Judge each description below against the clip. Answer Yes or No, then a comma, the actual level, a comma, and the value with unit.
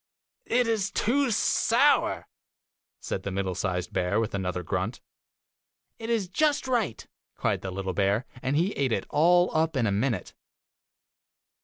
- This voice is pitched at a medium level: No, low, 130 Hz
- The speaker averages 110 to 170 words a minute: Yes, average, 150 wpm